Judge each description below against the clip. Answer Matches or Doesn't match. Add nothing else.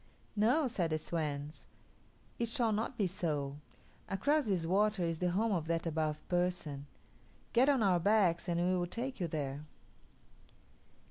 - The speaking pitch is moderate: Matches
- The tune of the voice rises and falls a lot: Doesn't match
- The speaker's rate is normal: Matches